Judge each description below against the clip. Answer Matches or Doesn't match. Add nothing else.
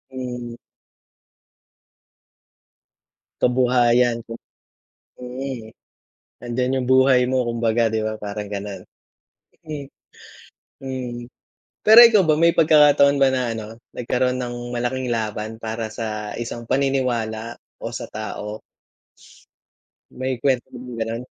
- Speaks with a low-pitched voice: Matches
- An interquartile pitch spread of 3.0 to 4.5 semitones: Doesn't match